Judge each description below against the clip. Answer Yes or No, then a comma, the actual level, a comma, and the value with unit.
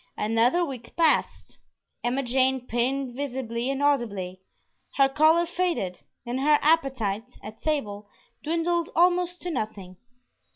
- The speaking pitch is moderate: No, very high, 265 Hz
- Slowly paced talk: Yes, slow, 120 wpm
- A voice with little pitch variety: No, wide, 5.5 semitones